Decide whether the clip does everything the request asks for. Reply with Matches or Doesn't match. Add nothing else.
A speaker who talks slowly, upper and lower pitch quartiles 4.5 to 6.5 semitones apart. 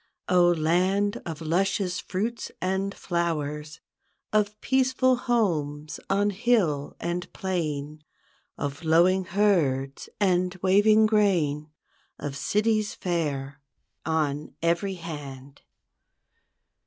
Matches